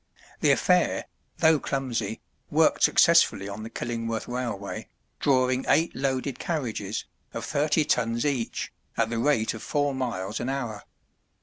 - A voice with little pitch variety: No, average, 3.5 semitones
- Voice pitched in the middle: No, low, 125 Hz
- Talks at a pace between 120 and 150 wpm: Yes, slow, 135 wpm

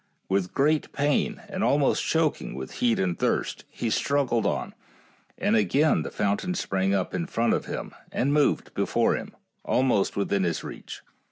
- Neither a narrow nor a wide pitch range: No, wide, 6.9 semitones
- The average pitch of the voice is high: No, low, 120 Hz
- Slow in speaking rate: No, average, 170 wpm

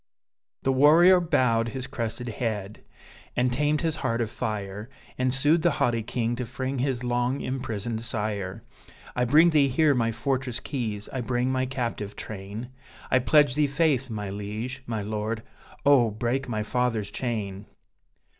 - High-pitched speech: No, low, 120 Hz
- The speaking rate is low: No, average, 155 wpm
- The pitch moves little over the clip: No, average, 3.5 semitones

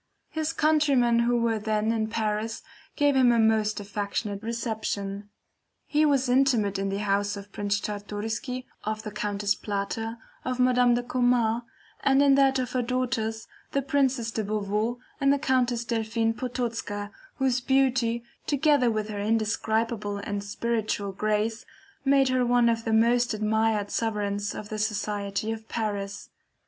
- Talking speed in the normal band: Yes, average, 150 wpm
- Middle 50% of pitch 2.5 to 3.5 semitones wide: Yes, average, 3.1 semitones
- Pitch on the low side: No, high, 225 Hz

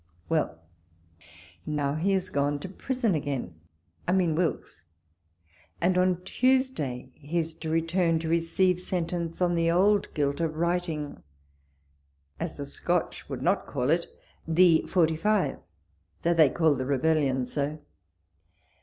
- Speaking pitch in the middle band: Yes, medium, 165 Hz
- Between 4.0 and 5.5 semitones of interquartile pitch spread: No, average, 3.5 semitones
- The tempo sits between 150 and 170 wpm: No, average, 140 wpm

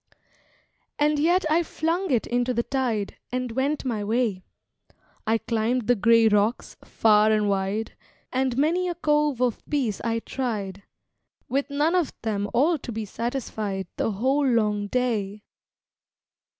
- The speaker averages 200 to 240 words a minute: No, average, 145 wpm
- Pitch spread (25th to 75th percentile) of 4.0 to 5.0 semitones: Yes, average, 4.7 semitones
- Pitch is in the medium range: No, high, 240 Hz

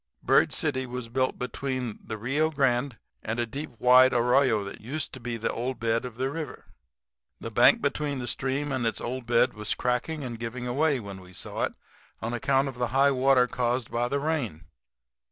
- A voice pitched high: No, low, 125 Hz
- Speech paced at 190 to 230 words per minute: Yes, average, 200 wpm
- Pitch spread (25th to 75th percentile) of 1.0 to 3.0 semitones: Yes, narrow, 2.5 semitones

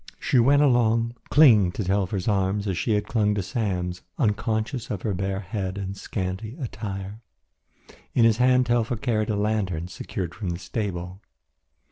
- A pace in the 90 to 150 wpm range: No, average, 160 wpm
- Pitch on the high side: No, low, 105 Hz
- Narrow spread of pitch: No, average, 3.3 semitones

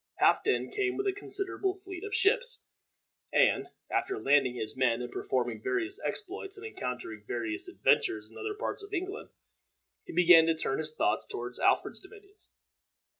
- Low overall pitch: No, very high, 365 Hz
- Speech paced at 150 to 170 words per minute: Yes, average, 160 wpm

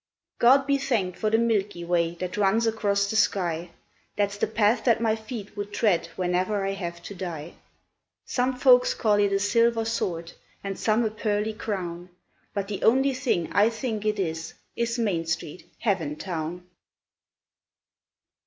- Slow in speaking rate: No, average, 160 wpm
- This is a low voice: No, high, 205 Hz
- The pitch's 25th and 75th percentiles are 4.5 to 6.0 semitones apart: No, average, 4.1 semitones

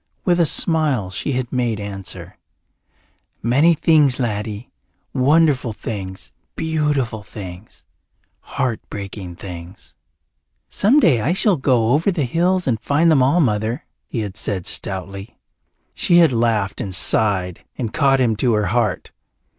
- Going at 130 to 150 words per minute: Yes, average, 140 wpm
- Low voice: Yes, low, 120 Hz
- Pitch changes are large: Yes, wide, 6.4 semitones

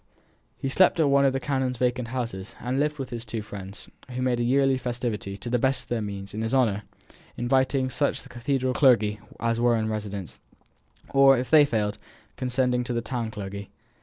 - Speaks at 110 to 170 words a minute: No, fast, 205 wpm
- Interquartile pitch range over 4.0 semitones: No, average, 3.3 semitones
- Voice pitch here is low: Yes, low, 125 Hz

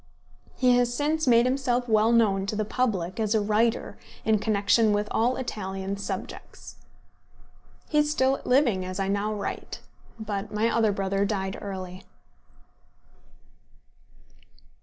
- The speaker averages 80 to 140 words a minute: Yes, slow, 135 wpm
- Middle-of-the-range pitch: No, high, 215 Hz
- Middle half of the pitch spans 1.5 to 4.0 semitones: Yes, average, 3.4 semitones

